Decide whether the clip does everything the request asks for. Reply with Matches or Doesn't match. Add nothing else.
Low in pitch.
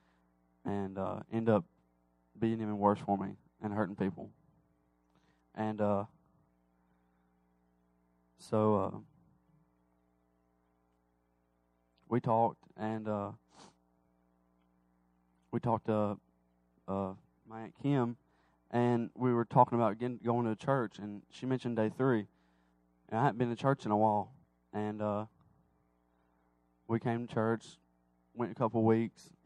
Matches